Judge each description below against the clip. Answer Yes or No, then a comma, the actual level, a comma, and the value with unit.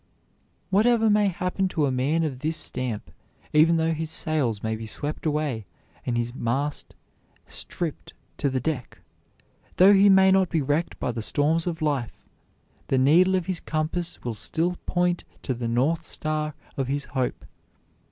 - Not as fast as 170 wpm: Yes, average, 160 wpm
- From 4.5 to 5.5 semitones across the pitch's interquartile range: Yes, average, 4.9 semitones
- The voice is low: No, medium, 155 Hz